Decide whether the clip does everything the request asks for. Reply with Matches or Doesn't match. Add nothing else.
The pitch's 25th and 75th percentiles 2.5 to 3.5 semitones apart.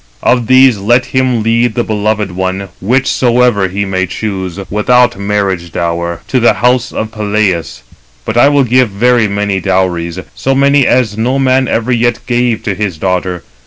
Doesn't match